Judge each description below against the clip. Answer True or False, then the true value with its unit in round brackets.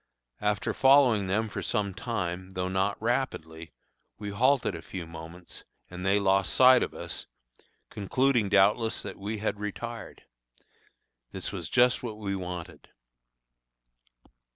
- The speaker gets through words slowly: True (130 wpm)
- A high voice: False (100 Hz)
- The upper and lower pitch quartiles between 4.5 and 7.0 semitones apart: False (3.8 semitones)